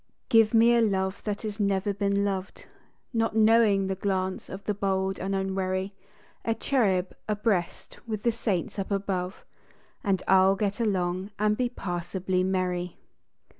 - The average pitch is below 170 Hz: No, high, 195 Hz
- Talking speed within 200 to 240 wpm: No, average, 155 wpm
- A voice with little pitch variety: Yes, narrow, 2.1 semitones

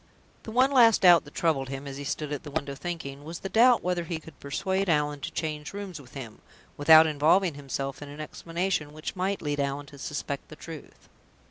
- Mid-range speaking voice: Yes, medium, 155 Hz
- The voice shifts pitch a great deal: No, average, 3.8 semitones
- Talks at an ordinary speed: No, fast, 215 wpm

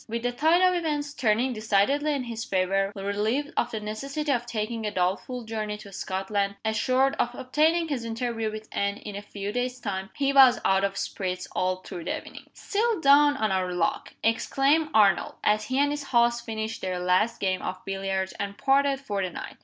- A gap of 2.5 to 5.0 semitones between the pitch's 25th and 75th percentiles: No, wide, 5.4 semitones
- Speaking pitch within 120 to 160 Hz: No, high, 225 Hz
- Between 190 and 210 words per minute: Yes, average, 200 wpm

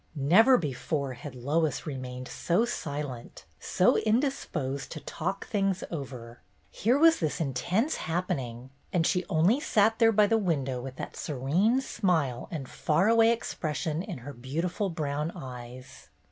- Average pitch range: No, wide, 7.0 semitones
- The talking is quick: No, average, 145 wpm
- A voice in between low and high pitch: Yes, medium, 160 Hz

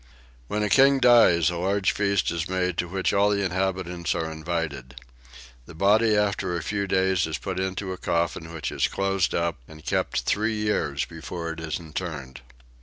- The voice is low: Yes, very low, 90 Hz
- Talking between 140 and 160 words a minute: No, average, 180 wpm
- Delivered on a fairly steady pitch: No, average, 3.3 semitones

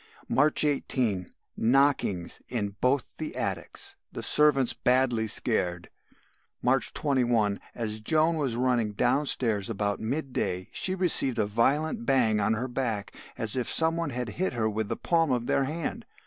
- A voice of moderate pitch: No, low, 125 Hz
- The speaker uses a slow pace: No, average, 155 wpm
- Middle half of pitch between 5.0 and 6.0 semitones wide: No, average, 4.6 semitones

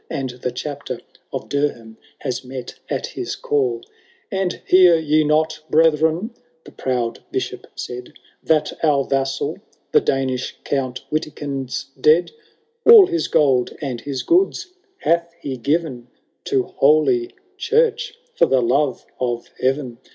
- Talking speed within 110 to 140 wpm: Yes, slow, 135 wpm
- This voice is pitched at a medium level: Yes, medium, 150 Hz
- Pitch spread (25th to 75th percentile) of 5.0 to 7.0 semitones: Yes, wide, 5.4 semitones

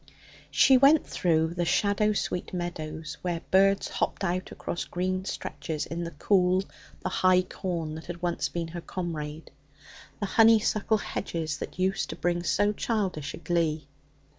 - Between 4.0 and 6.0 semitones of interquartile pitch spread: No, average, 3.0 semitones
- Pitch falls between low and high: Yes, medium, 175 Hz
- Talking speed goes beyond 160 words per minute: No, average, 155 wpm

